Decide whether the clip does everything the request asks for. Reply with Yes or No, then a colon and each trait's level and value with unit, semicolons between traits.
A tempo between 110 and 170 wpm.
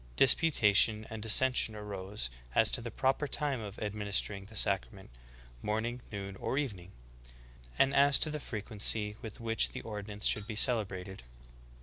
Yes: average, 160 wpm